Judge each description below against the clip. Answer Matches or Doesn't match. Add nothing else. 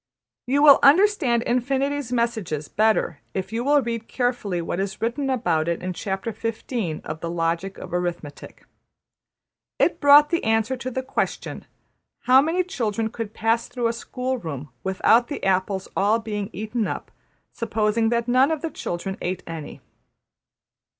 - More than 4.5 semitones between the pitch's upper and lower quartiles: Matches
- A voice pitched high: Matches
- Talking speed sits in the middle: Matches